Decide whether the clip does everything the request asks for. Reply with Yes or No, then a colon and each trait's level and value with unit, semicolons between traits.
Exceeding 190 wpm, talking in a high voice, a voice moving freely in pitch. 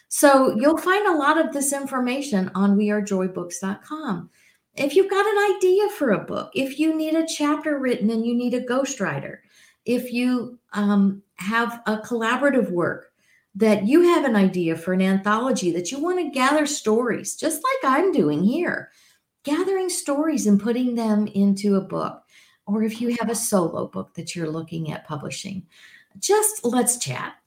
No: average, 170 wpm; high, 240 Hz; wide, 6.9 semitones